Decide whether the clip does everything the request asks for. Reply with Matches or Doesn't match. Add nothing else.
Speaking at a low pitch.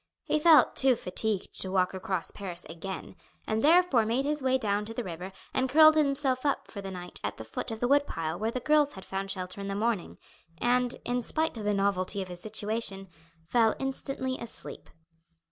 Doesn't match